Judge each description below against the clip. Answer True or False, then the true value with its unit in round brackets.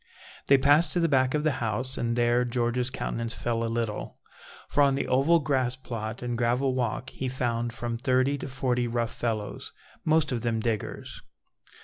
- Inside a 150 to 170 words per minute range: False (185 wpm)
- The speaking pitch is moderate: False (125 Hz)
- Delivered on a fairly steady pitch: True (2.2 semitones)